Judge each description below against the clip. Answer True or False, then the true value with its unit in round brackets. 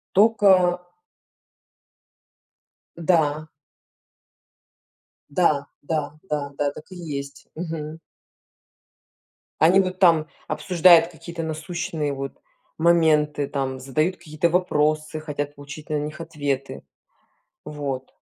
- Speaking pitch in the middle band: True (155 Hz)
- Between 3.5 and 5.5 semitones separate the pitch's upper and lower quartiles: False (2.9 semitones)